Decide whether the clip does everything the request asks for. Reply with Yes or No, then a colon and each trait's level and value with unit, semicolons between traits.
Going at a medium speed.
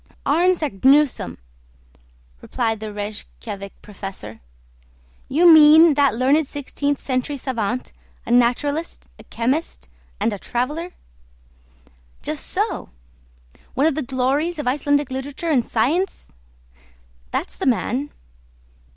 No: slow, 110 wpm